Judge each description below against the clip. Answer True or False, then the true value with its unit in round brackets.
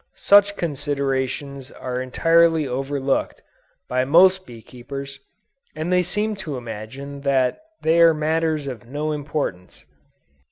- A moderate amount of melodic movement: True (3.7 semitones)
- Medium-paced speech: False (120 wpm)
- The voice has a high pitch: False (140 Hz)